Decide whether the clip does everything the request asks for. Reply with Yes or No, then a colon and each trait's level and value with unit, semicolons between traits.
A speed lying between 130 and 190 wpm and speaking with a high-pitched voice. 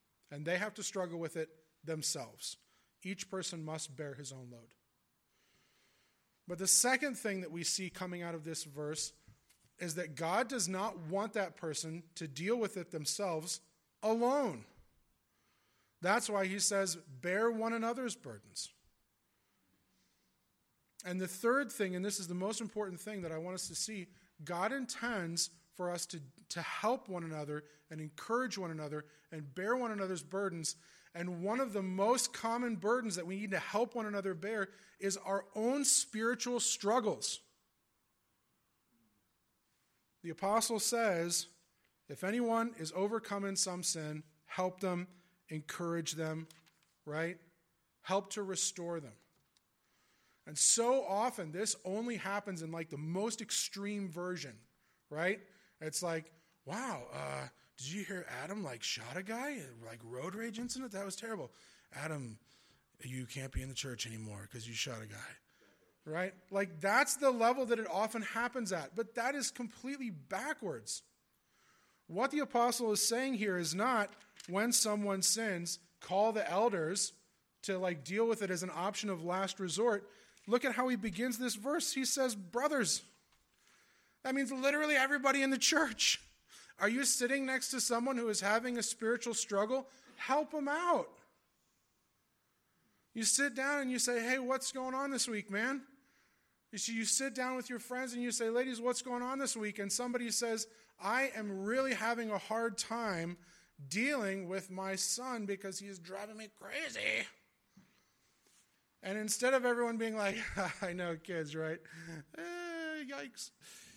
Yes: average, 160 wpm; high, 200 Hz